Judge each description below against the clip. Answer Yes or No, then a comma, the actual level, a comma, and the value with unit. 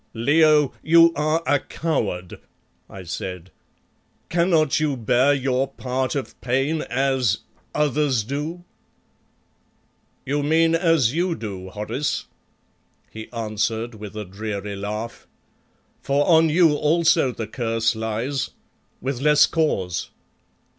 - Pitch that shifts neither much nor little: No, wide, 5.7 semitones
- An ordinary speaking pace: No, slow, 115 wpm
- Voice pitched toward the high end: No, low, 135 Hz